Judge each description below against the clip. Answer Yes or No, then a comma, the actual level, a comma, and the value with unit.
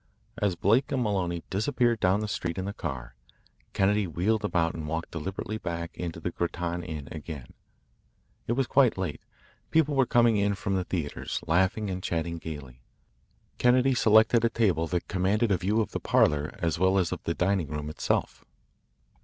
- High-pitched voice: No, very low, 95 Hz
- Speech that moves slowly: No, average, 180 wpm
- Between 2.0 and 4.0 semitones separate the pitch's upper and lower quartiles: No, average, 4.6 semitones